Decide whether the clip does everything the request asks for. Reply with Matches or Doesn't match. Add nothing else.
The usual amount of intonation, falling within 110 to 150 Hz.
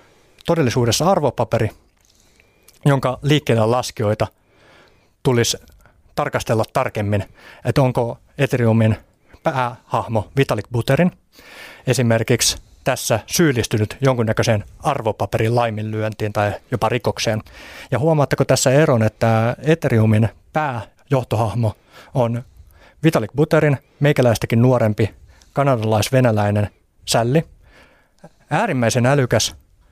Matches